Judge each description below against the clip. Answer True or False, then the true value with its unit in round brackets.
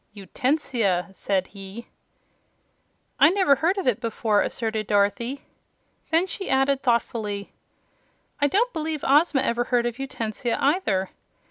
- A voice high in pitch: True (240 Hz)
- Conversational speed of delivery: False (125 wpm)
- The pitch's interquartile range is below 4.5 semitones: False (5.5 semitones)